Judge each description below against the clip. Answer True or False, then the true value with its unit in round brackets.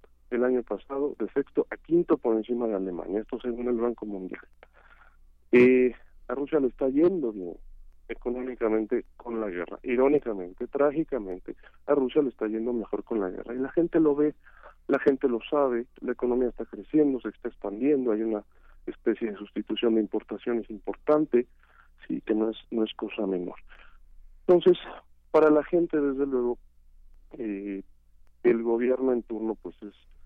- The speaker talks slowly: False (165 wpm)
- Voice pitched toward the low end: True (120 Hz)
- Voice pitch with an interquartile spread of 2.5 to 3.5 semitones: False (4.6 semitones)